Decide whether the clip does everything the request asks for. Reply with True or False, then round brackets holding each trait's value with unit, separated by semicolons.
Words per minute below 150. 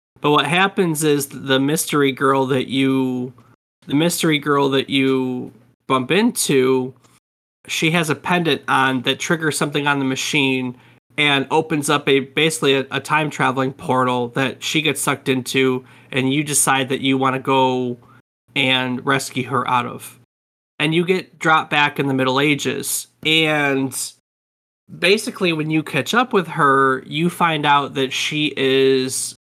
False (160 wpm)